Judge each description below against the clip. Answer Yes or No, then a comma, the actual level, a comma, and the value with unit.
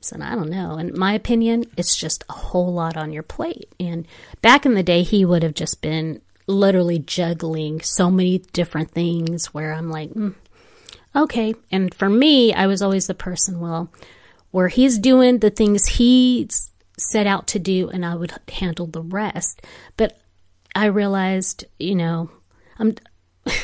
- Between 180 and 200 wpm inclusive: No, average, 170 wpm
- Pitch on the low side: No, medium, 185 Hz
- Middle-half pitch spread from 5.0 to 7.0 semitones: No, average, 4.2 semitones